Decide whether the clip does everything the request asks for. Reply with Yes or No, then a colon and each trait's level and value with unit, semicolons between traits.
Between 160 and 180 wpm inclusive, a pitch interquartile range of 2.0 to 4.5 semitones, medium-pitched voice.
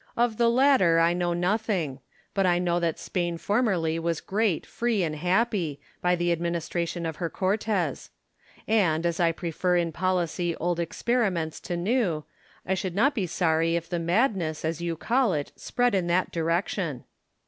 Yes: average, 170 wpm; average, 3.2 semitones; medium, 175 Hz